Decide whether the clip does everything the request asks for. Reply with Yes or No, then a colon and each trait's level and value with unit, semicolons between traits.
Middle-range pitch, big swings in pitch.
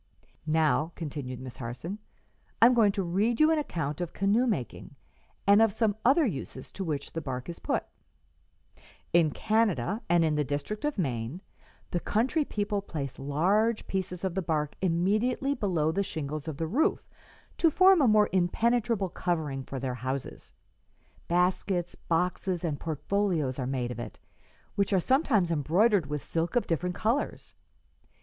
Yes: medium, 175 Hz; wide, 6.1 semitones